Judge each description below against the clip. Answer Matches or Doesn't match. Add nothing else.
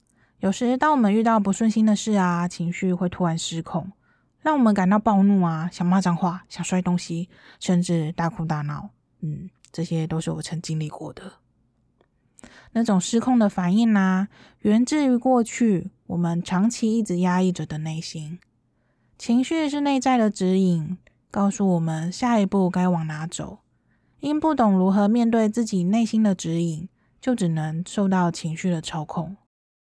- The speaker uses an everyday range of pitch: Matches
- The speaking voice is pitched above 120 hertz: Matches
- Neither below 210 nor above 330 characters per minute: Matches